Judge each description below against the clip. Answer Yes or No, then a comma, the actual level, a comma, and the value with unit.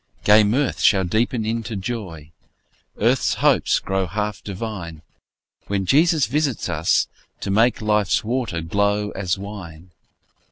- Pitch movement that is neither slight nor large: Yes, average, 3.5 semitones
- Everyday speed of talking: No, slow, 125 wpm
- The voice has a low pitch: Yes, low, 105 Hz